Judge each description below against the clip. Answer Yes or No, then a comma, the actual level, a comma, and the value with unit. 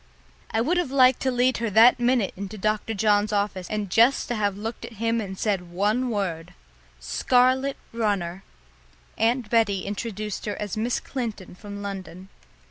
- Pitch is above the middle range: Yes, high, 215 Hz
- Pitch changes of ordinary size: Yes, average, 3.2 semitones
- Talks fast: No, average, 165 wpm